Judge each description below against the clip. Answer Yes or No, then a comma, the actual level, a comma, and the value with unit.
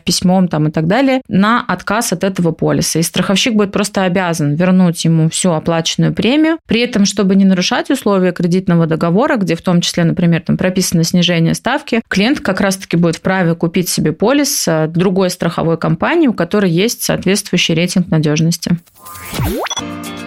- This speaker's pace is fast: Yes, fast, 165 wpm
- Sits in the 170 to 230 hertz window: Yes, medium, 185 Hz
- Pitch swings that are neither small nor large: Yes, average, 3.5 semitones